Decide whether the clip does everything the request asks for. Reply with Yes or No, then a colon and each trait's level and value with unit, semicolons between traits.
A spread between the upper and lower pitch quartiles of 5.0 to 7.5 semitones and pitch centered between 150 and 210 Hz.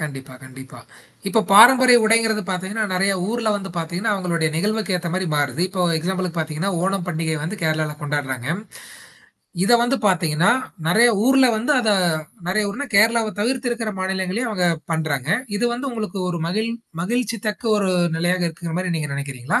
Yes: average, 5.3 semitones; medium, 185 Hz